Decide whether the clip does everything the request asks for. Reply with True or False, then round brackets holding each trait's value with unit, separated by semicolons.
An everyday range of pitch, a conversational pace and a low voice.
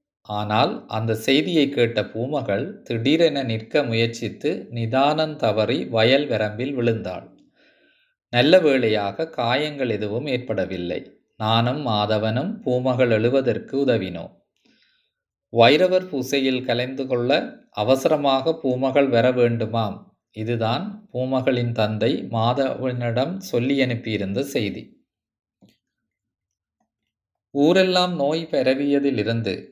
True (4.2 semitones; 85 wpm; 125 Hz)